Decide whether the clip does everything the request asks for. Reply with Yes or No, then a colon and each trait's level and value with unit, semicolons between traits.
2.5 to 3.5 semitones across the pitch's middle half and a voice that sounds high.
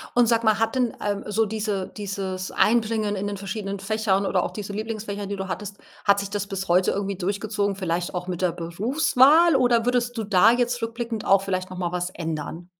Yes: average, 3.0 semitones; high, 205 Hz